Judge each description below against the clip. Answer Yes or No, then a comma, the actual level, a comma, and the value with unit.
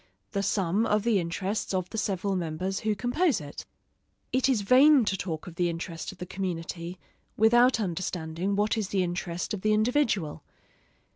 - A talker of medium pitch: No, high, 195 Hz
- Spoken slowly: No, average, 170 wpm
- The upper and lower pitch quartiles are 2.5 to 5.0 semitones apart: Yes, average, 3.9 semitones